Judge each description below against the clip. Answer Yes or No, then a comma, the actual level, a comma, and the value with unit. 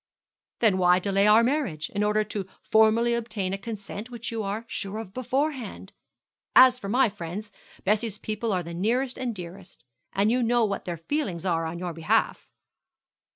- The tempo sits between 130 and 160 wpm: No, average, 175 wpm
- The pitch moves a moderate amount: Yes, average, 3.9 semitones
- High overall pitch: Yes, high, 210 Hz